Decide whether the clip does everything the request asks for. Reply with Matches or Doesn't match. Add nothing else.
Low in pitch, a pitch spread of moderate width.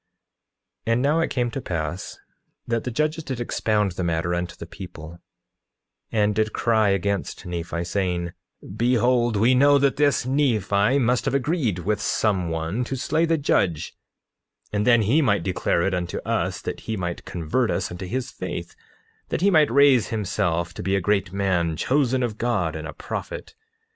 Doesn't match